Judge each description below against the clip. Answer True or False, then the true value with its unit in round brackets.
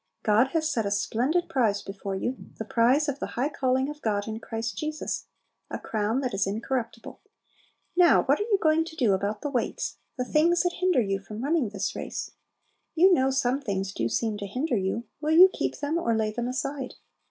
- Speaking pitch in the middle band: False (250 Hz)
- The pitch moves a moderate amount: False (6.3 semitones)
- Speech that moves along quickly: True (210 wpm)